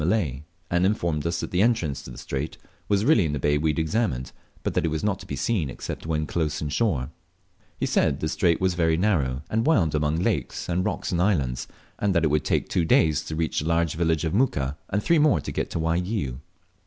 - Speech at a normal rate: No, fast, 240 wpm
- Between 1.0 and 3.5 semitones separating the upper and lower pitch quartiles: No, average, 4.0 semitones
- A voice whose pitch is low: Yes, very low, 80 Hz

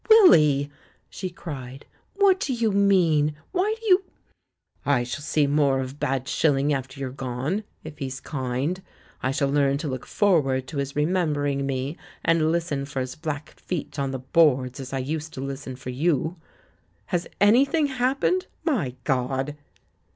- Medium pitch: Yes, medium, 145 Hz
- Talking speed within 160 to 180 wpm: Yes, average, 165 wpm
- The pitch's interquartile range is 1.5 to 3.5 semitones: No, average, 4.8 semitones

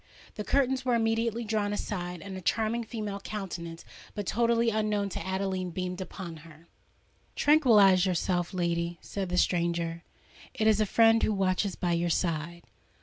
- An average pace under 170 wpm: Yes, average, 155 wpm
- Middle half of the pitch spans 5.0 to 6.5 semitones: No, average, 3.9 semitones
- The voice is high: Yes, high, 195 Hz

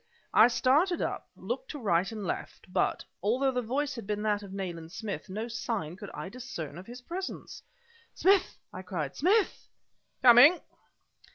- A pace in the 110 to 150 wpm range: No, average, 165 wpm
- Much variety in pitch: Yes, wide, 6.2 semitones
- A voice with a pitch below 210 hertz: No, high, 230 Hz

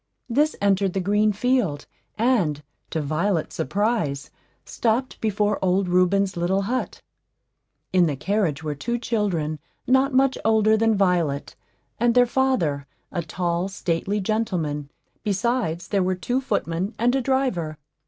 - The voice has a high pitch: Yes, high, 195 Hz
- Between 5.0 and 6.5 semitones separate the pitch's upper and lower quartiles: Yes, average, 5.3 semitones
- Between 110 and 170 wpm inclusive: Yes, slow, 135 wpm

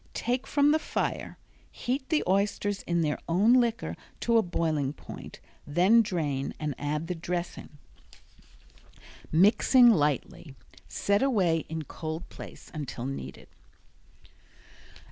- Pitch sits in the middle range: Yes, medium, 175 Hz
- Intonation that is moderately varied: No, wide, 7.0 semitones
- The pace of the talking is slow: Yes, slow, 120 wpm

